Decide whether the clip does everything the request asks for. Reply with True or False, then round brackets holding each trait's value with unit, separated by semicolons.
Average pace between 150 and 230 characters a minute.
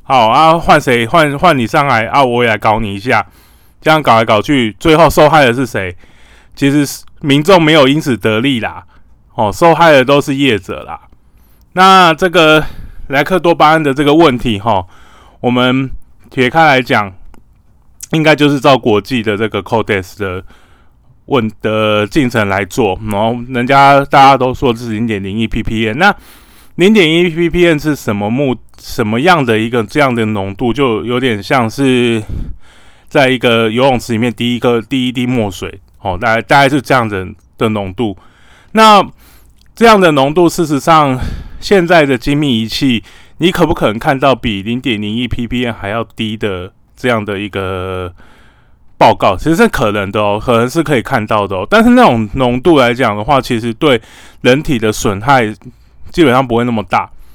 False (260 characters per minute)